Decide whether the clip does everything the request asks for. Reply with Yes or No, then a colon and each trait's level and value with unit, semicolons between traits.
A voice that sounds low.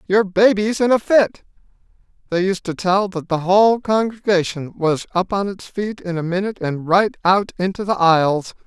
No: high, 190 Hz